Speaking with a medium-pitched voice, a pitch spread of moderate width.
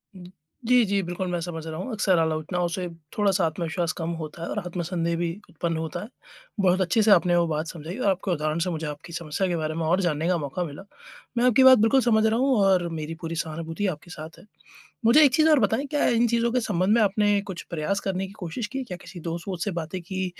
Yes: medium, 180 Hz; average, 4.0 semitones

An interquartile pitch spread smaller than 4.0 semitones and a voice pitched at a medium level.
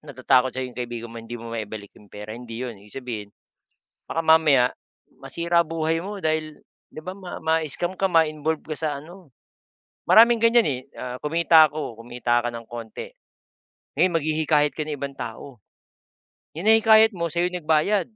No: wide, 5.5 semitones; medium, 155 Hz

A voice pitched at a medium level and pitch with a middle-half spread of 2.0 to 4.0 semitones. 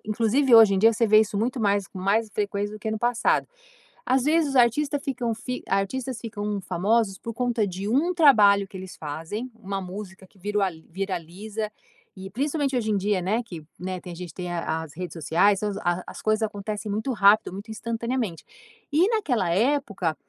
No: high, 210 Hz; average, 3.7 semitones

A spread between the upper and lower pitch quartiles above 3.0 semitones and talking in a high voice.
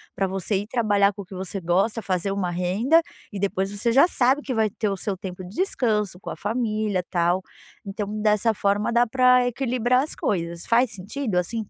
Yes: average, 3.8 semitones; high, 205 Hz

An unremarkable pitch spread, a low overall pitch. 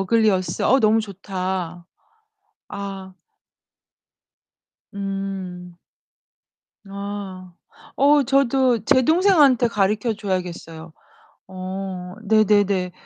No: average, 3.3 semitones; high, 195 Hz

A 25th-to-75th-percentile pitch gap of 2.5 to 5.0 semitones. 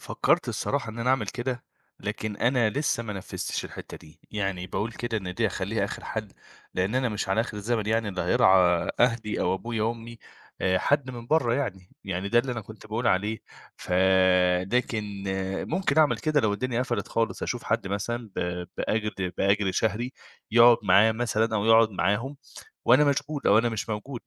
Yes: average, 3.3 semitones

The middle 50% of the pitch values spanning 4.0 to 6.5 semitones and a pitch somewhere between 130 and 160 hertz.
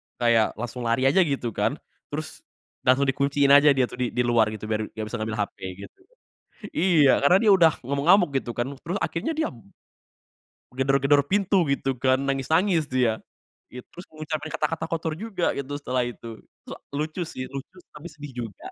Yes: average, 4.3 semitones; medium, 140 Hz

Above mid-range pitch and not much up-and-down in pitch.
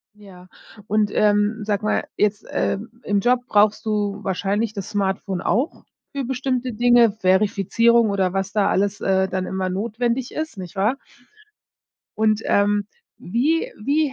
No: high, 210 Hz; average, 3.1 semitones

